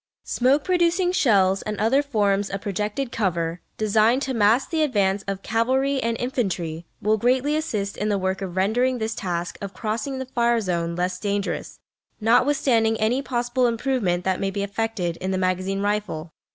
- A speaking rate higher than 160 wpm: Yes, average, 170 wpm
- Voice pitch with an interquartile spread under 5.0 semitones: Yes, average, 4.6 semitones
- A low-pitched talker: No, high, 215 Hz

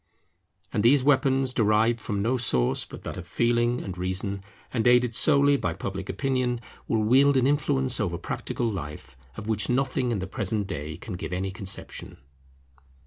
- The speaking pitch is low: Yes, low, 115 Hz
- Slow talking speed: No, average, 170 wpm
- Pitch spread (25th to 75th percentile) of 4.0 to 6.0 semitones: Yes, average, 4.8 semitones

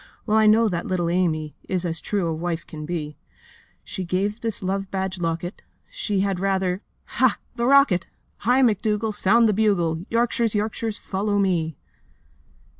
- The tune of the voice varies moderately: Yes, average, 3.7 semitones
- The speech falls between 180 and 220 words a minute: No, average, 165 wpm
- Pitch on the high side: Yes, high, 195 Hz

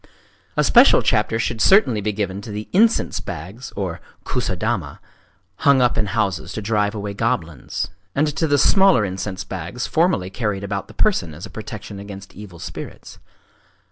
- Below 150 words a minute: No, average, 155 wpm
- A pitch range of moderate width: Yes, average, 3.9 semitones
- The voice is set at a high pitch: No, low, 105 Hz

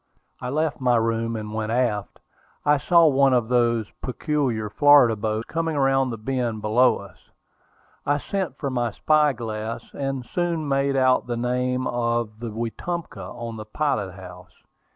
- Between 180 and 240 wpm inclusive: No, average, 160 wpm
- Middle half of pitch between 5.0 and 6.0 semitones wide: No, average, 3.8 semitones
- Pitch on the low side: Yes, low, 125 Hz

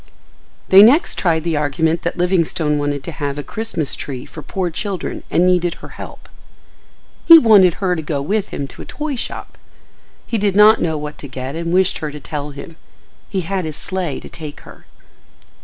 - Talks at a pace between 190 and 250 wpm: Yes, average, 195 wpm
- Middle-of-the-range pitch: Yes, medium, 170 Hz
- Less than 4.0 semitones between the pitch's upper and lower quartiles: No, average, 4.3 semitones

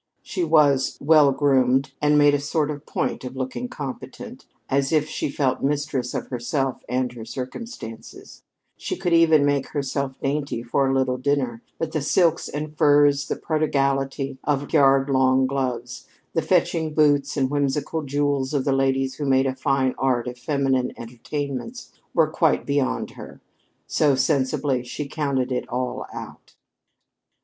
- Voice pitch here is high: No, medium, 140 Hz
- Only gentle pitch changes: Yes, narrow, 2.1 semitones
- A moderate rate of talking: Yes, average, 155 wpm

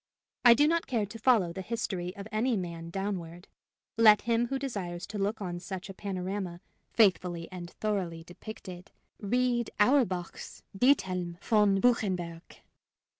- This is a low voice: No, high, 195 Hz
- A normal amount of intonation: Yes, average, 4.3 semitones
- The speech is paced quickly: No, average, 140 wpm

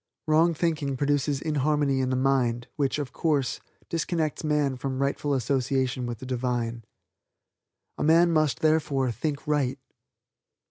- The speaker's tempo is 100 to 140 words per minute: Yes, slow, 135 wpm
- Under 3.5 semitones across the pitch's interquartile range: Yes, average, 2.9 semitones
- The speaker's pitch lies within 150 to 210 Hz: No, medium, 140 Hz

